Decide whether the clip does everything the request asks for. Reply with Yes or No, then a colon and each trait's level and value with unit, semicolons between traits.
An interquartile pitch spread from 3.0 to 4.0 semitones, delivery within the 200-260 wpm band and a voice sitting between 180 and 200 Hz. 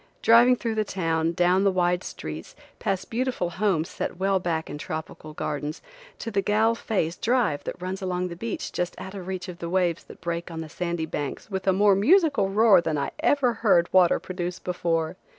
Yes: average, 3.5 semitones; fast, 205 wpm; medium, 185 Hz